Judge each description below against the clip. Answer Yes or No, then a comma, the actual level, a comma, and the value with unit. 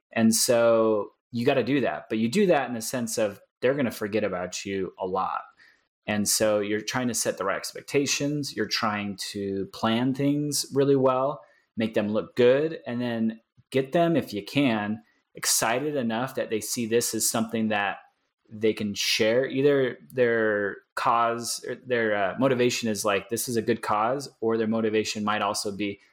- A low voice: Yes, low, 115 Hz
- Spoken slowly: No, average, 190 wpm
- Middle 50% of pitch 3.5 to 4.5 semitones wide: No, average, 3.0 semitones